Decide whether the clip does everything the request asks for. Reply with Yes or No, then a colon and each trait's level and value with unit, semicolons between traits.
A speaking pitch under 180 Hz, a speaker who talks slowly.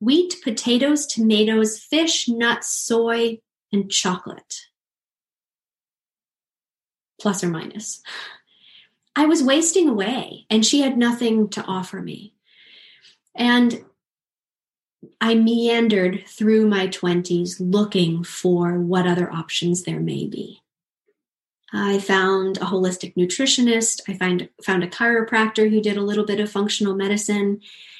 No: high, 210 Hz; slow, 115 wpm